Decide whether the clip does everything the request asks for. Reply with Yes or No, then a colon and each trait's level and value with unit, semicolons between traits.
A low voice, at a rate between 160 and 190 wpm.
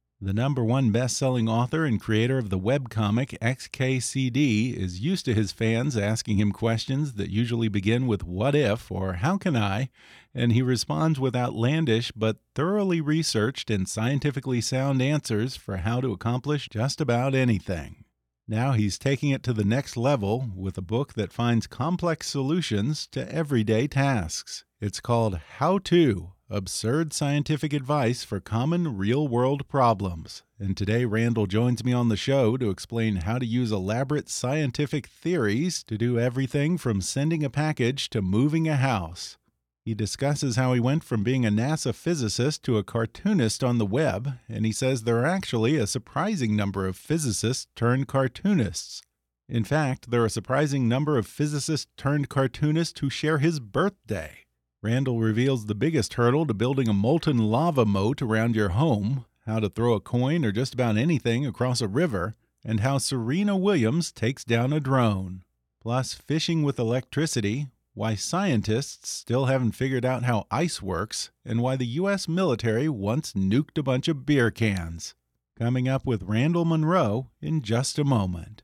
Yes: low, 125 Hz; average, 165 wpm